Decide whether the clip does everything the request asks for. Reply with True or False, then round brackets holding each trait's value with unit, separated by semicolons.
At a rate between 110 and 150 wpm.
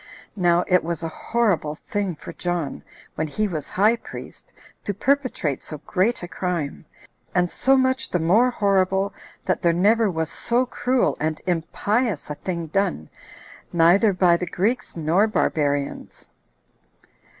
True (145 wpm)